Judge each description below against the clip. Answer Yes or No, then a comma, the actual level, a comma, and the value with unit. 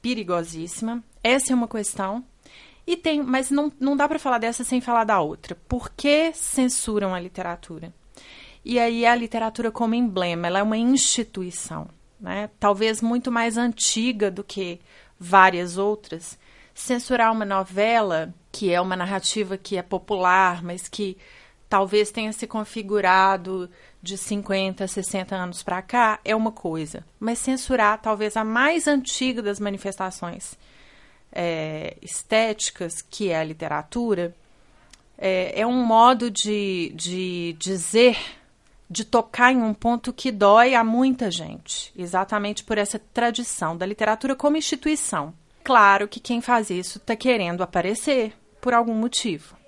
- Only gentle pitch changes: No, average, 4.3 semitones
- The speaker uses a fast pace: No, average, 140 wpm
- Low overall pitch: No, high, 215 Hz